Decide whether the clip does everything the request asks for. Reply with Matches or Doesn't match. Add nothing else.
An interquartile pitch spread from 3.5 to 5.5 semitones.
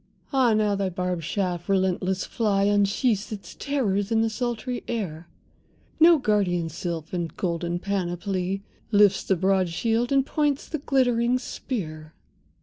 Matches